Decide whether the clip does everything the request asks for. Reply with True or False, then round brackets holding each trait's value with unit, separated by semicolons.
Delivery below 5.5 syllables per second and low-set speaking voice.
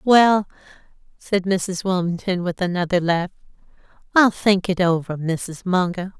False (4.2 syllables/s; 185 Hz)